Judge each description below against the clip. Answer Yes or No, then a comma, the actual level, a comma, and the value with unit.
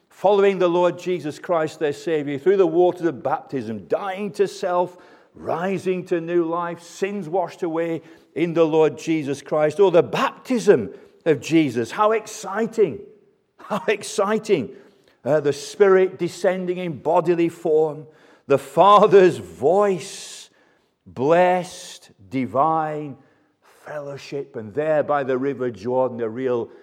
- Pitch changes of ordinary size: Yes, average, 4.2 semitones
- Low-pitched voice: No, medium, 170 Hz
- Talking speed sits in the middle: No, slow, 130 wpm